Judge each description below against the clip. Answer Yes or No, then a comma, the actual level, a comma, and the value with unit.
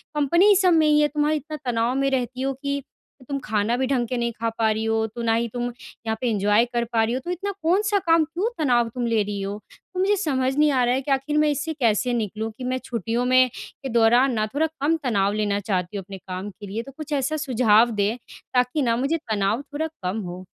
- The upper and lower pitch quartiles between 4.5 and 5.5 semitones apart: Yes, average, 4.9 semitones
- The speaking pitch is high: Yes, high, 245 Hz